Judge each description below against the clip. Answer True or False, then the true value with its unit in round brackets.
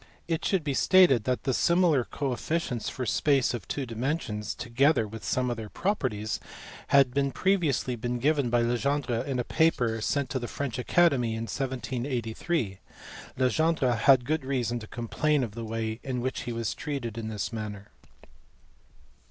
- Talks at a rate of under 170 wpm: True (160 wpm)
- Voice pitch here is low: True (125 Hz)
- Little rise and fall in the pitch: False (3.6 semitones)